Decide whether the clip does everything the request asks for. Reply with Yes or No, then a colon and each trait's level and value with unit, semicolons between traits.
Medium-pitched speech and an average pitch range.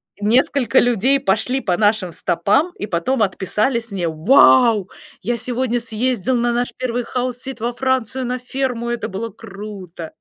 No: high, 235 Hz; average, 3.7 semitones